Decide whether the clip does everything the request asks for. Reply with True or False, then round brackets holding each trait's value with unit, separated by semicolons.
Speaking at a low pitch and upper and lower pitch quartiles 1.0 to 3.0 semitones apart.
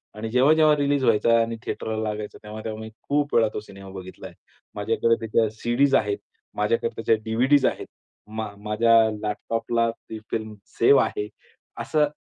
False (115 Hz; 3.6 semitones)